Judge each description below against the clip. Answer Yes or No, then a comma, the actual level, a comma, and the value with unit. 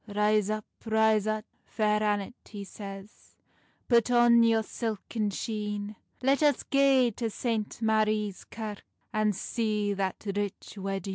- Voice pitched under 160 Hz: No, high, 215 Hz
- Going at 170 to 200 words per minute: No, slow, 135 wpm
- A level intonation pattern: Yes, narrow, 1.7 semitones